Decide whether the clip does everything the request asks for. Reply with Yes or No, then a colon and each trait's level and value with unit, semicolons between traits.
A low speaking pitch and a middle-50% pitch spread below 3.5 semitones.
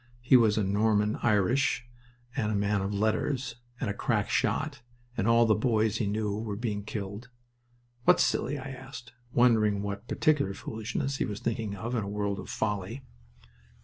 Yes: low, 110 Hz; average, 2.9 semitones